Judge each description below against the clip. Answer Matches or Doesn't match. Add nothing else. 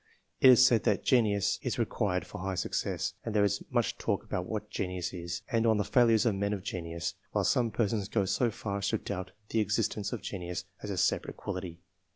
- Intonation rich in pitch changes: Doesn't match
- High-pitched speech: Doesn't match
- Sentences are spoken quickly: Matches